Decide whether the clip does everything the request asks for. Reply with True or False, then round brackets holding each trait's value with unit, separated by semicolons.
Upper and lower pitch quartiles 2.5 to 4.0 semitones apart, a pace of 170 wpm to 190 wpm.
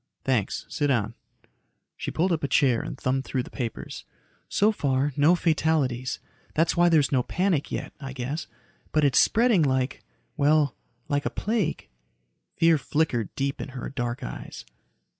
False (3.7 semitones; 160 wpm)